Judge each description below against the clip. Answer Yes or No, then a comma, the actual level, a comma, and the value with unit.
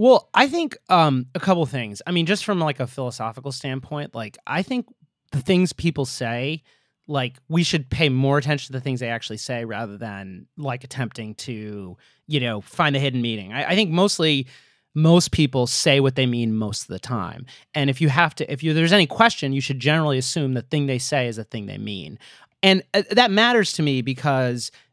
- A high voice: No, medium, 140 Hz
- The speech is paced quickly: Yes, fast, 215 wpm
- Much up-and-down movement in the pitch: No, average, 5.0 semitones